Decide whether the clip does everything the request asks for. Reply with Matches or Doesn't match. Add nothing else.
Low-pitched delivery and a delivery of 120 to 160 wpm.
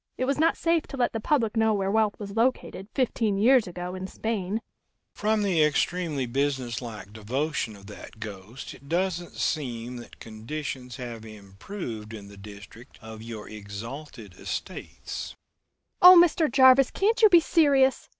Doesn't match